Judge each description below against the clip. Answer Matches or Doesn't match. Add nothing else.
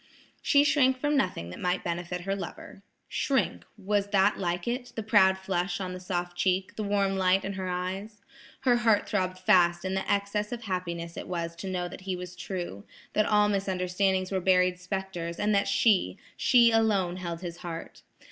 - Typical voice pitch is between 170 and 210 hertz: Matches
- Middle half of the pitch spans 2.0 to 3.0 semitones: Matches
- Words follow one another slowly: Doesn't match